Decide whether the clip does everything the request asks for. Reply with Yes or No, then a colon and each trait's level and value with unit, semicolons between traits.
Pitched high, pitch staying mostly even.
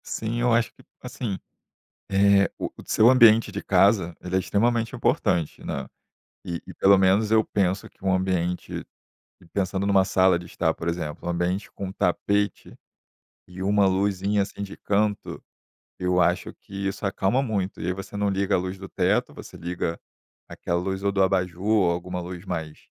No: very low, 95 Hz; narrow, 2.1 semitones